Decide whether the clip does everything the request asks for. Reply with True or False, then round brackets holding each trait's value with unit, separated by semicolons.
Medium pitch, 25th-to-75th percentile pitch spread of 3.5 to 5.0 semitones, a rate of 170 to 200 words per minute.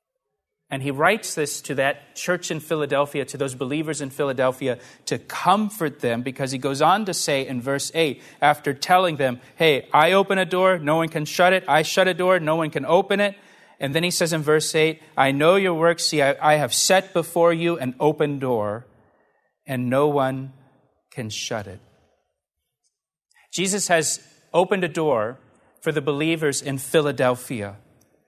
True (150 Hz; 4.1 semitones; 180 wpm)